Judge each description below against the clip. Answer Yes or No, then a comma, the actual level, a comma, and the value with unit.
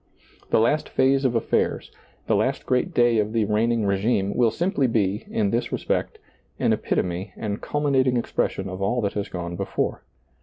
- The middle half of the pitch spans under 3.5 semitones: No, average, 4.0 semitones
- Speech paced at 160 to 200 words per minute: Yes, average, 175 wpm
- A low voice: Yes, low, 110 Hz